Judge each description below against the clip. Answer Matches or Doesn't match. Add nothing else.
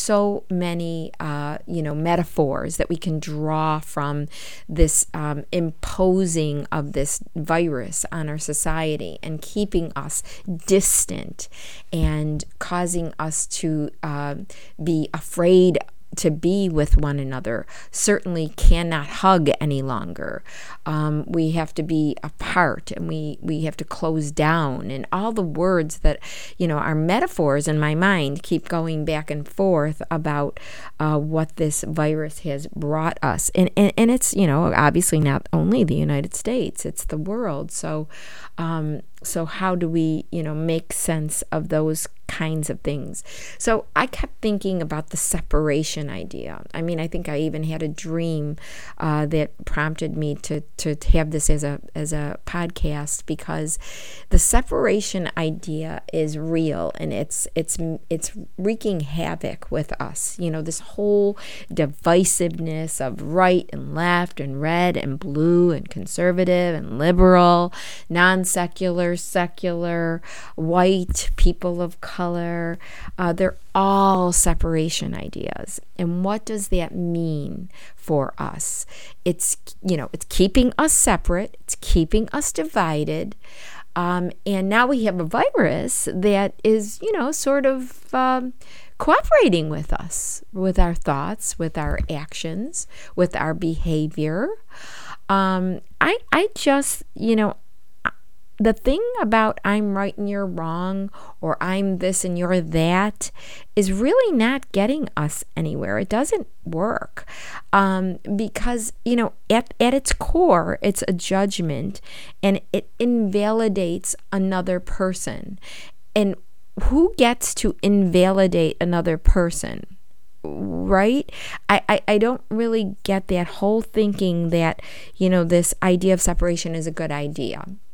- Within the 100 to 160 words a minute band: Matches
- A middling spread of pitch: Matches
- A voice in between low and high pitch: Matches